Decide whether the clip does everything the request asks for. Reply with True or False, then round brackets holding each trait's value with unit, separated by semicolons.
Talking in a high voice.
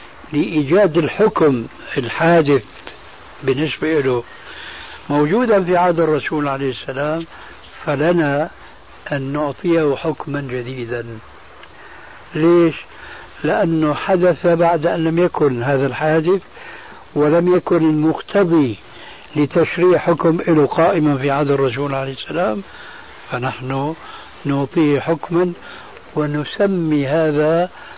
False (155 Hz)